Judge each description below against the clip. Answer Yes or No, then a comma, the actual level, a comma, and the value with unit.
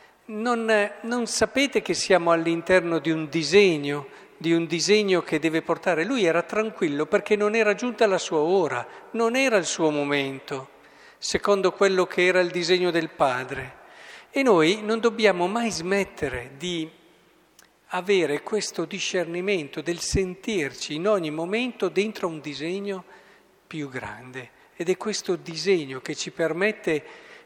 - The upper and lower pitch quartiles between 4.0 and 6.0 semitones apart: Yes, average, 4.3 semitones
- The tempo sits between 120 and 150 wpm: Yes, average, 140 wpm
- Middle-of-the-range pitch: Yes, medium, 180 Hz